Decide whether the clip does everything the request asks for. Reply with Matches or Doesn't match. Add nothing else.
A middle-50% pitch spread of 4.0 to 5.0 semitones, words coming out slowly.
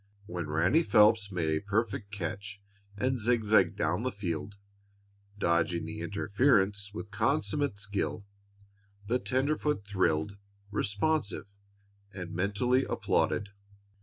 Matches